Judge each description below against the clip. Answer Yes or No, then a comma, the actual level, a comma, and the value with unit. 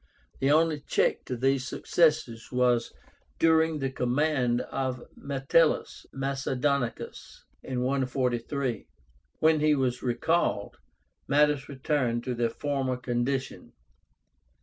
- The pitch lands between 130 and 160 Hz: Yes, low, 135 Hz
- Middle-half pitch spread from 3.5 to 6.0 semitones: No, average, 2.9 semitones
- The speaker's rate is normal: No, slow, 100 wpm